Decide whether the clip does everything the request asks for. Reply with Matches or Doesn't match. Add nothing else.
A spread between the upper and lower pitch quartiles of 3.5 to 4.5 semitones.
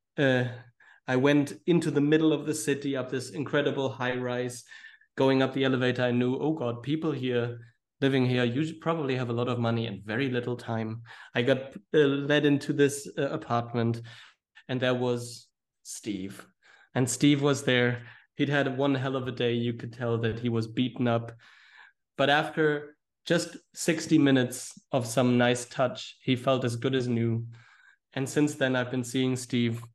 Doesn't match